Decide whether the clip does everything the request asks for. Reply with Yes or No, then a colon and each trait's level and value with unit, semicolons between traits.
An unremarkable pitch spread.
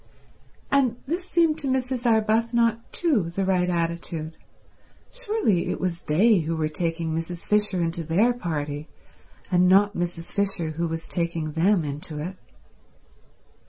No: wide, 5.8 semitones